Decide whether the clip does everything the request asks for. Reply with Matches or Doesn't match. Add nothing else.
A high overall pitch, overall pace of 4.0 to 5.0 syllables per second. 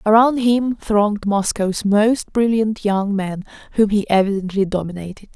Matches